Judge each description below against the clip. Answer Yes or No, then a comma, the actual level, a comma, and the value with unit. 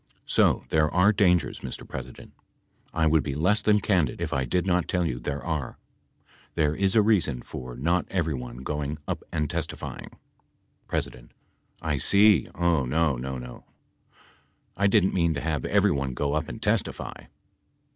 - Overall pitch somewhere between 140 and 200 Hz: No, very low, 80 Hz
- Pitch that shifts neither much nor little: Yes, average, 4.6 semitones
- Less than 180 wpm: Yes, average, 160 wpm